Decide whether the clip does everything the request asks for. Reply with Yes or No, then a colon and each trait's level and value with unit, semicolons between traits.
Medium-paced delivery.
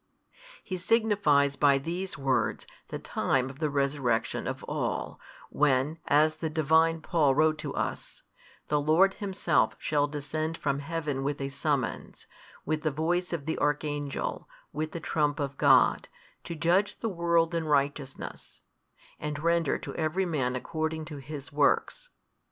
Yes: average, 150 wpm